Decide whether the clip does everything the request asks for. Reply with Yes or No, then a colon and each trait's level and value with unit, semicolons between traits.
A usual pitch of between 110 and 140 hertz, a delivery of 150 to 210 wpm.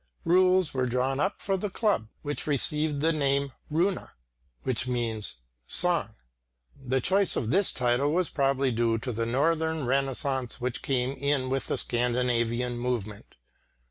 No: low, 135 Hz; average, 140 wpm